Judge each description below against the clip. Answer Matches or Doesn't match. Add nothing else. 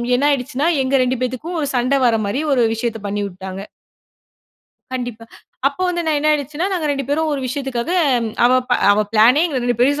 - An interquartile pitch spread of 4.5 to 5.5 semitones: Doesn't match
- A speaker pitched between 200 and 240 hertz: Doesn't match